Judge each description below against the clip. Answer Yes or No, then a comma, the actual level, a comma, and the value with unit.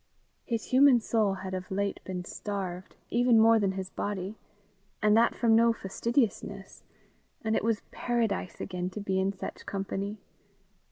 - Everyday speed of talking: Yes, average, 155 wpm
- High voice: Yes, high, 205 Hz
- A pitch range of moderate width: Yes, average, 3.1 semitones